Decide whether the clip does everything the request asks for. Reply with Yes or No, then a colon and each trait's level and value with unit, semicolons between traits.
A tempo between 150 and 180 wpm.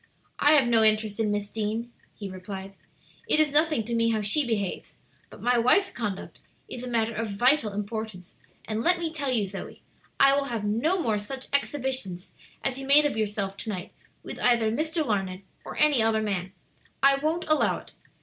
No: average, 195 wpm